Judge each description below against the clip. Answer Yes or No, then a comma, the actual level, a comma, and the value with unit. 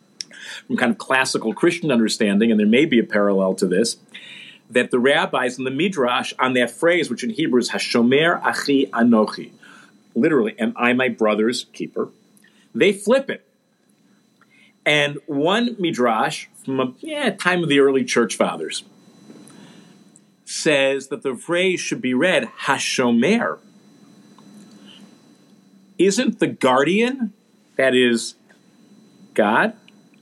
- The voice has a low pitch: No, medium, 145 Hz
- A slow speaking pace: Yes, slow, 130 wpm